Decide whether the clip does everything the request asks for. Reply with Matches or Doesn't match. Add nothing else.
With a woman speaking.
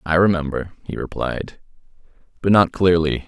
Doesn't match